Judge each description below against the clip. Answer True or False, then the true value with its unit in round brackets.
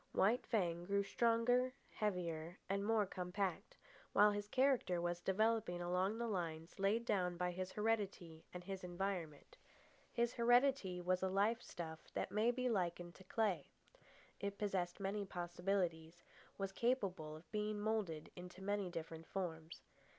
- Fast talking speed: False (145 wpm)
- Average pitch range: True (3.4 semitones)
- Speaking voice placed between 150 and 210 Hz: True (190 Hz)